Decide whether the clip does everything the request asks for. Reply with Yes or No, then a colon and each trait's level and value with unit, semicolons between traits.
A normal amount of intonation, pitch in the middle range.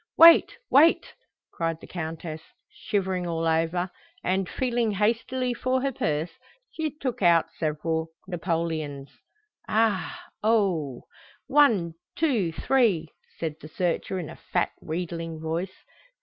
No: wide, 6.1 semitones; medium, 180 Hz